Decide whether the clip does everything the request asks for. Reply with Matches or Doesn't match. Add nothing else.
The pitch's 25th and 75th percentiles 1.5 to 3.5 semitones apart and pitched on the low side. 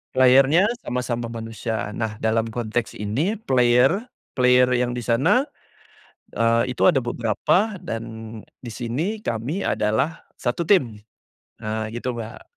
Matches